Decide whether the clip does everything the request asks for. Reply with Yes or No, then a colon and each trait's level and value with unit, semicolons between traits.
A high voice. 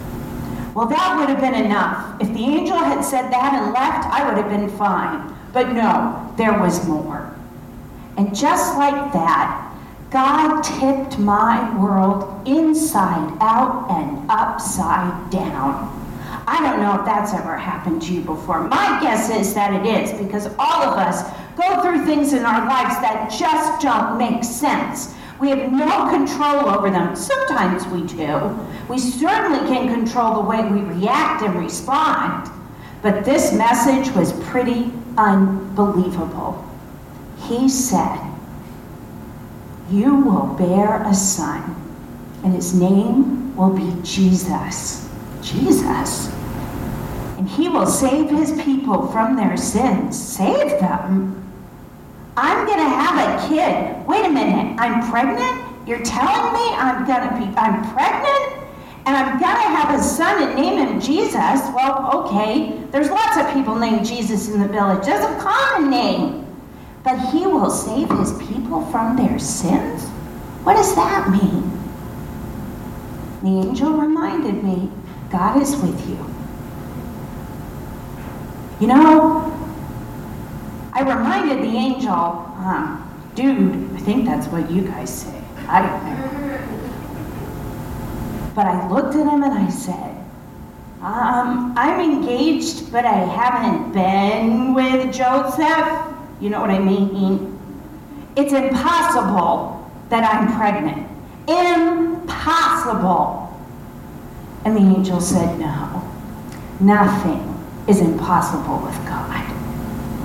Yes: high, 245 Hz